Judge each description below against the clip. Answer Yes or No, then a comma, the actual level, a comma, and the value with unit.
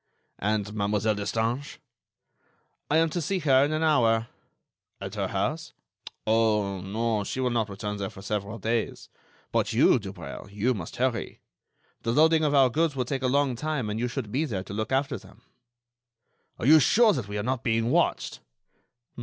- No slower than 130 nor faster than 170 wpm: No, average, 180 wpm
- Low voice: Yes, low, 115 Hz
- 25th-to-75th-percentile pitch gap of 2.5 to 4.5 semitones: No, average, 5.0 semitones